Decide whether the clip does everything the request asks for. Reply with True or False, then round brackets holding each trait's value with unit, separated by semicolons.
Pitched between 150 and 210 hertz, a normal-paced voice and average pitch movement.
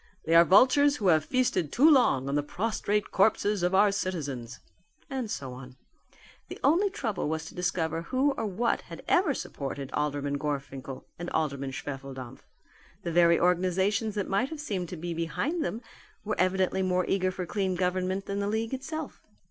False (185 Hz; 175 wpm; 5.7 semitones)